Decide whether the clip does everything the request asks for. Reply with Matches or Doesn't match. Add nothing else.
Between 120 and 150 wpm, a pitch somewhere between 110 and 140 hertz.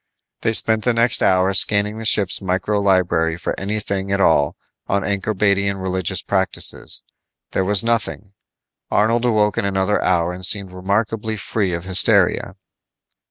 Doesn't match